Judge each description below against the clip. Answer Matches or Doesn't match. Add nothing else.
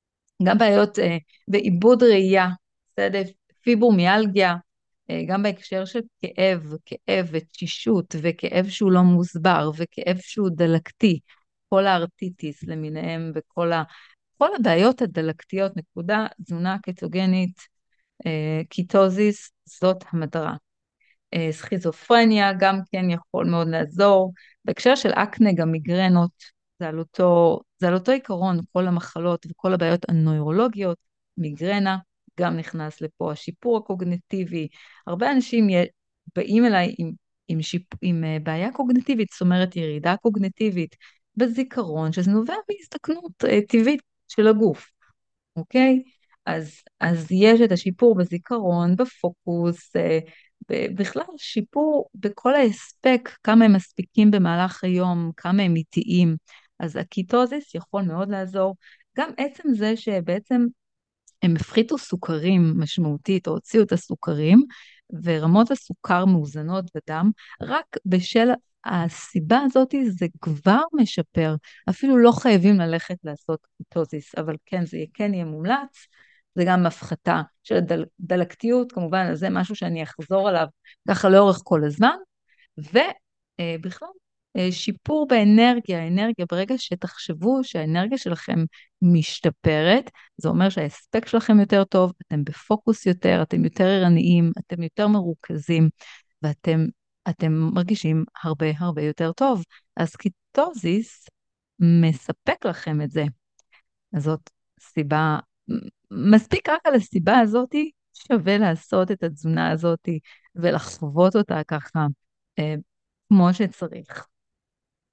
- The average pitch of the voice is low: Doesn't match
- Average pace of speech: Matches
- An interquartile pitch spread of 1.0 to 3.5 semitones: Doesn't match